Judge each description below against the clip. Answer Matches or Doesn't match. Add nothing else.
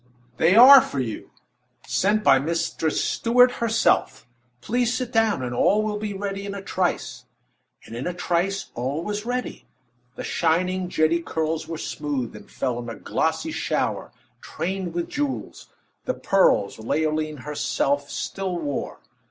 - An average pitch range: Doesn't match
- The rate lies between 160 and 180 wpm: Doesn't match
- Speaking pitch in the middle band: Matches